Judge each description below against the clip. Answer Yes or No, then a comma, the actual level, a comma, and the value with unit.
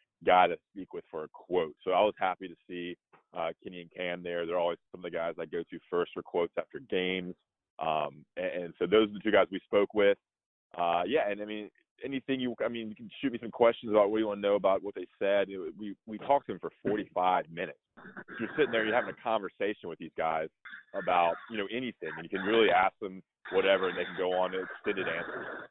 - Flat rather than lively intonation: No, average, 3.5 semitones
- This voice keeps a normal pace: No, fast, 250 wpm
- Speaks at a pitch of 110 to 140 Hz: No, low, 100 Hz